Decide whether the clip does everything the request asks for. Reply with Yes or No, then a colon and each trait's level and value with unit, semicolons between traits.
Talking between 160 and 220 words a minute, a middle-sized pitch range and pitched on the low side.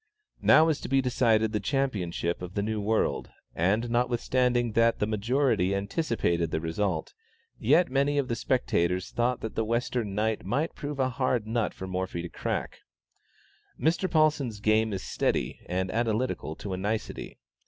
Yes: average, 165 wpm; average, 4.6 semitones; low, 110 Hz